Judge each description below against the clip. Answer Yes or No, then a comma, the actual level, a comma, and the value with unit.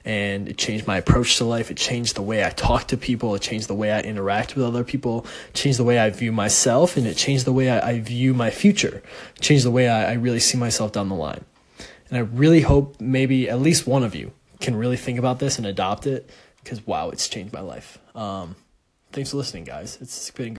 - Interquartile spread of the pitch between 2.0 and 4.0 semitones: Yes, average, 3.3 semitones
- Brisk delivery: Yes, fast, 240 wpm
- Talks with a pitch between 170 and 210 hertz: No, low, 120 Hz